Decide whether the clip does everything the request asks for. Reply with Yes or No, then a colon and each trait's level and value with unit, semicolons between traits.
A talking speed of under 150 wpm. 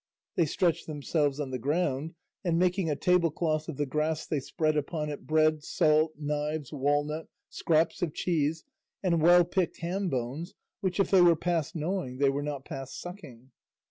No: average, 170 wpm